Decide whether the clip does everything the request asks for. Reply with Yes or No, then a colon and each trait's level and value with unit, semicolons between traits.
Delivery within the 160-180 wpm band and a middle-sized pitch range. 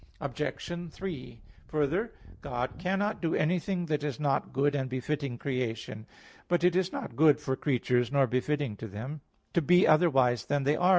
Yes: average, 170 wpm; average, 5.0 semitones